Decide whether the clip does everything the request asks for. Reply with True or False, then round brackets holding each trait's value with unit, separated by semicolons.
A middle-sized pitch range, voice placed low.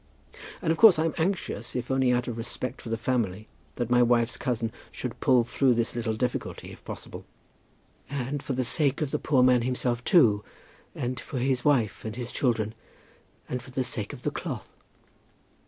False (2.3 semitones; 125 Hz)